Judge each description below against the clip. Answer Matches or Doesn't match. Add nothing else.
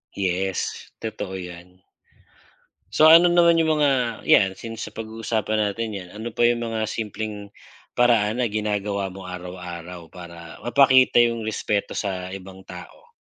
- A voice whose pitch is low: Matches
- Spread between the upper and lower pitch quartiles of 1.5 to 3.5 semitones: Doesn't match